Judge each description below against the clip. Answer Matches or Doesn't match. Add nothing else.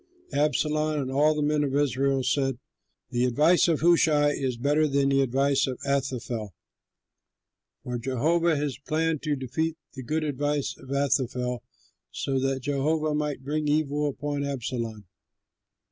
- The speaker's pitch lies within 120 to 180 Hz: Matches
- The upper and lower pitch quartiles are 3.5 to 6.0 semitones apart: Doesn't match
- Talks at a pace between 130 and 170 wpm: Matches